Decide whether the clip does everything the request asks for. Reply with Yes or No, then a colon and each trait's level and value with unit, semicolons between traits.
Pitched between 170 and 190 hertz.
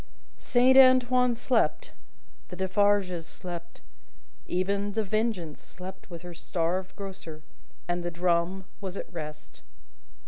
Yes: medium, 185 Hz